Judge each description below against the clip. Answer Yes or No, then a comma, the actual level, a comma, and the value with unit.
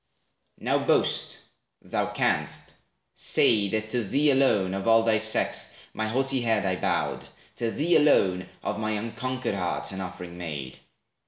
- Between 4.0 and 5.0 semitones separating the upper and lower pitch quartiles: Yes, average, 4.4 semitones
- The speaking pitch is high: No, low, 110 Hz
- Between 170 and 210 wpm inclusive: No, average, 150 wpm